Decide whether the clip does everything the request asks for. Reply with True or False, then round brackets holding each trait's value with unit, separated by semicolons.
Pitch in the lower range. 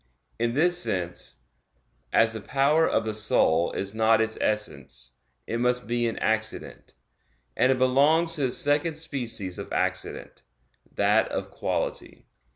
True (115 Hz)